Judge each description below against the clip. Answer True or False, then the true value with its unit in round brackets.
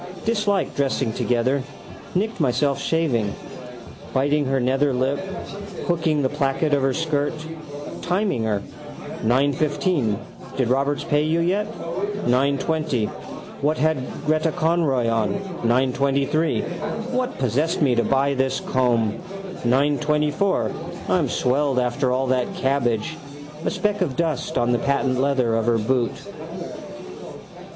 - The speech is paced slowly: True (120 wpm)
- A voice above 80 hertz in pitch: True (140 Hz)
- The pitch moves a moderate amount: True (3.7 semitones)